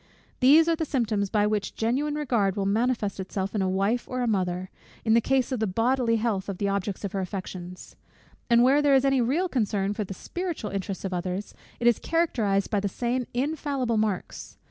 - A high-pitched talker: Yes, high, 220 Hz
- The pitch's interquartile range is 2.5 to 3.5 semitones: No, average, 4.6 semitones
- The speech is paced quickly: Yes, fast, 210 wpm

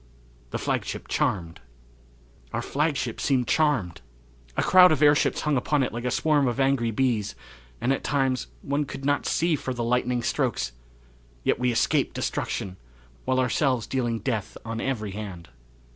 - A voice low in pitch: Yes, low, 125 Hz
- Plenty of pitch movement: No, average, 3.7 semitones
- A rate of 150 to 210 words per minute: Yes, average, 160 wpm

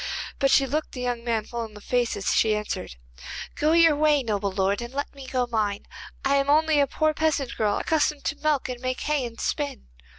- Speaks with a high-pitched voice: Yes, very high, 255 Hz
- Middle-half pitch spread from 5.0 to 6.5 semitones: No, average, 4.5 semitones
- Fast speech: Yes, fast, 225 wpm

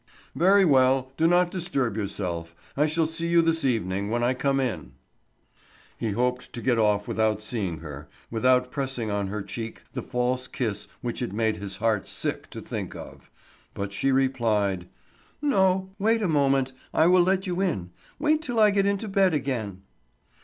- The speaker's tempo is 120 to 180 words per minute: Yes, average, 175 wpm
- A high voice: No, low, 130 Hz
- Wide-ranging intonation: Yes, wide, 8.1 semitones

